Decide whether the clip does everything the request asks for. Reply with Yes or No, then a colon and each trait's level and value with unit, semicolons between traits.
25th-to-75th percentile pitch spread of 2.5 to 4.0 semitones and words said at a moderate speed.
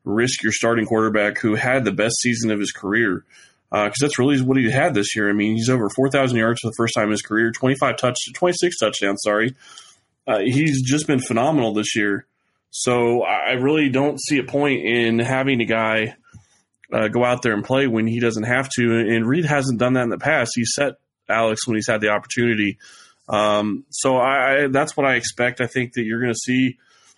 No: average, 3.1 semitones; fast, 220 wpm